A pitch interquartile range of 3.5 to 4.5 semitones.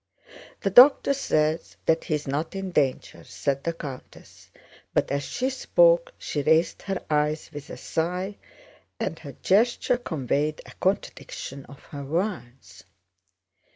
No: average, 5.2 semitones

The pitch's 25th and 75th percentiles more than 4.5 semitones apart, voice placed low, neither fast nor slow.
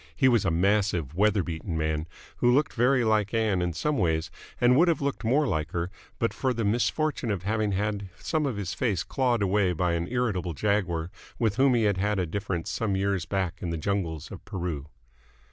No: average, 5.2 semitones; low, 100 Hz; fast, 210 wpm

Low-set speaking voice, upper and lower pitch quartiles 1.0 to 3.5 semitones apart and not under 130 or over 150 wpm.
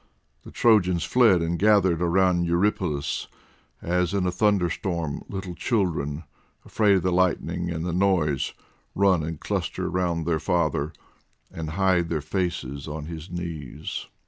Yes: very low, 85 Hz; narrow, 2.6 semitones; average, 140 wpm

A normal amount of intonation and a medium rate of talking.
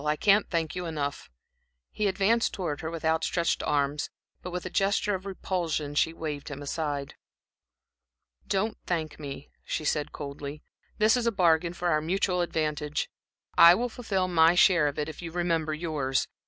Yes: average, 3.5 semitones; average, 170 wpm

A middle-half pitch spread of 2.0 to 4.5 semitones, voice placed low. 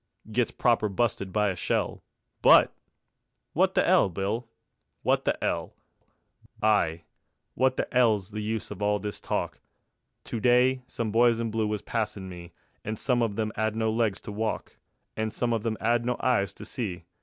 Yes: narrow, 2.4 semitones; low, 110 Hz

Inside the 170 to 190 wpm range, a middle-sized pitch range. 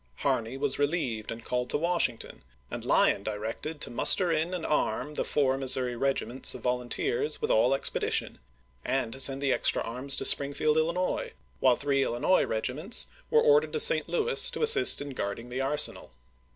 No: average, 180 wpm; wide, 6.2 semitones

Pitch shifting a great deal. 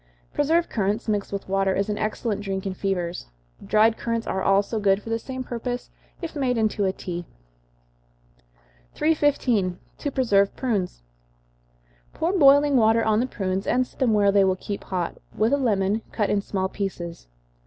No: average, 4.2 semitones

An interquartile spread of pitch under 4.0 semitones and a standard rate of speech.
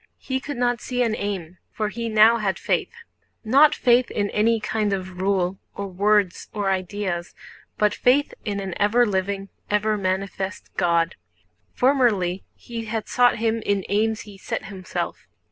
Yes: average, 3.2 semitones; average, 155 wpm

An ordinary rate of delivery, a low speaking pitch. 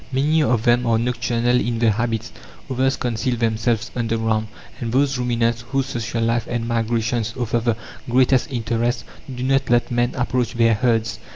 Yes: average, 165 wpm; low, 120 Hz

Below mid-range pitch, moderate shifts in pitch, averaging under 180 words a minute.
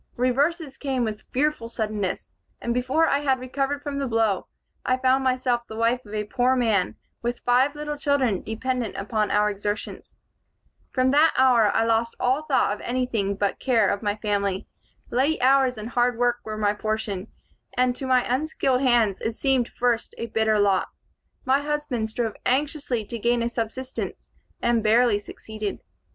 No: high, 240 Hz; average, 3.3 semitones; average, 170 wpm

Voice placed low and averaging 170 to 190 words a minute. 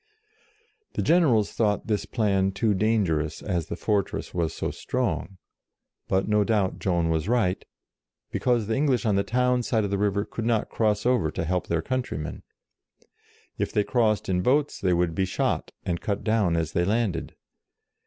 Yes: low, 105 Hz; average, 175 wpm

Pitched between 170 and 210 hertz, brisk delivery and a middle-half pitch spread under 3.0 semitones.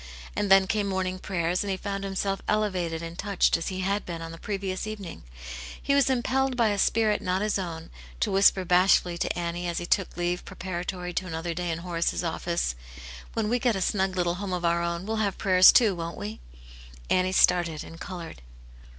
Yes: medium, 185 Hz; fast, 215 wpm; narrow, 2.6 semitones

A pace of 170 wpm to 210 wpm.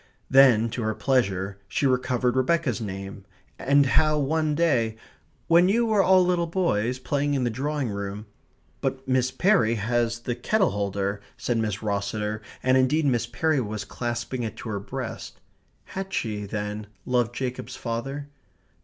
No: average, 160 wpm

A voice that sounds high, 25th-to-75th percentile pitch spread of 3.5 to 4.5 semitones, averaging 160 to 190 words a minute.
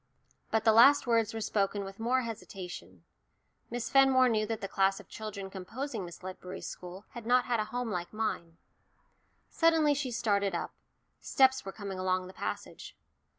Yes: high, 215 Hz; average, 4.2 semitones; average, 170 wpm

